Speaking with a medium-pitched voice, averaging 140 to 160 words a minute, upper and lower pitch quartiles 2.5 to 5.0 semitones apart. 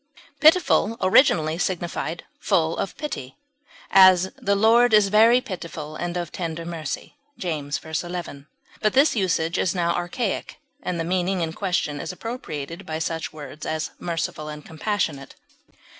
Yes: medium, 175 Hz; average, 145 wpm; average, 3.9 semitones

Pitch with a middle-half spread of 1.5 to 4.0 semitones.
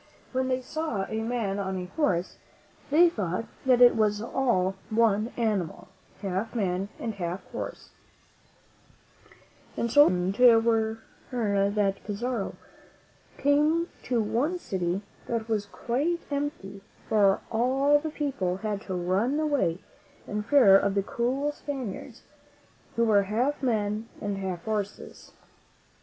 No: average, 4.6 semitones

